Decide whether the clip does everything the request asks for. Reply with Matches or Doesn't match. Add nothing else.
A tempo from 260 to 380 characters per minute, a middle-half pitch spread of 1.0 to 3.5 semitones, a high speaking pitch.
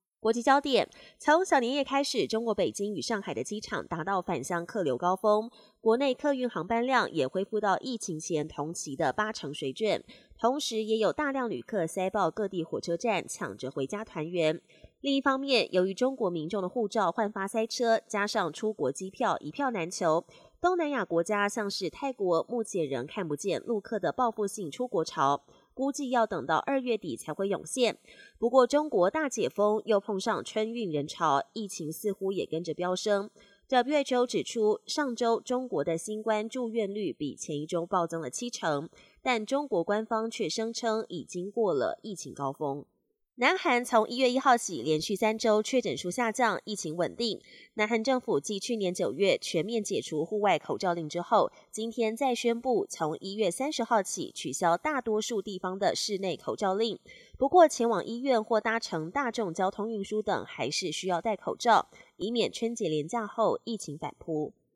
Doesn't match